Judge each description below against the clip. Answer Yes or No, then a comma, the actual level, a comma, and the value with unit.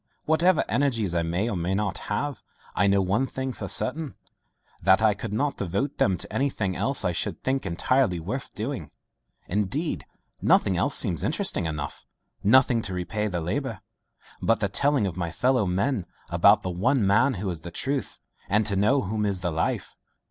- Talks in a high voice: No, low, 105 Hz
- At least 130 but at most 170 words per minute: No, average, 185 wpm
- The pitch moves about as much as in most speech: No, wide, 6.2 semitones